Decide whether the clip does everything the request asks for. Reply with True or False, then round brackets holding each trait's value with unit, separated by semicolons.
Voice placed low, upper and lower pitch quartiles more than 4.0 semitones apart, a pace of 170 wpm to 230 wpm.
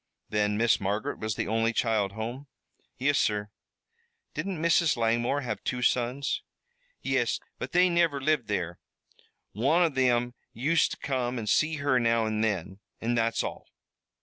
False (120 Hz; 4.4 semitones; 155 wpm)